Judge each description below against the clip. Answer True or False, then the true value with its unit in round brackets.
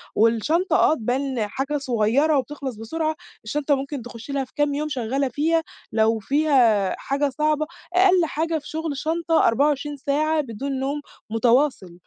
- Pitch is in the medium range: False (280 Hz)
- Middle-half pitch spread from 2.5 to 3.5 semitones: False (4.2 semitones)